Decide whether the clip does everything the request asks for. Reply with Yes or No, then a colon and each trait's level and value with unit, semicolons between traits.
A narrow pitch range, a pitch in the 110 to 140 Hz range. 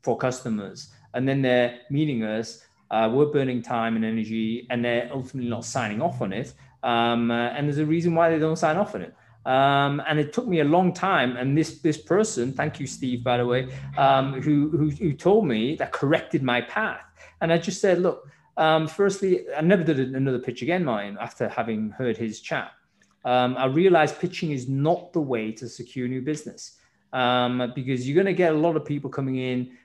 No: average, 4.4 semitones; low, 135 Hz